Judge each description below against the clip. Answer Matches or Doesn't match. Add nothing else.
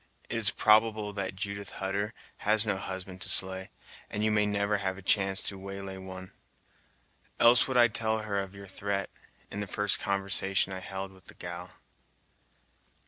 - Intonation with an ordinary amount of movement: Doesn't match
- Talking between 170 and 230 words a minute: Matches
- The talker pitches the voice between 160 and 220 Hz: Doesn't match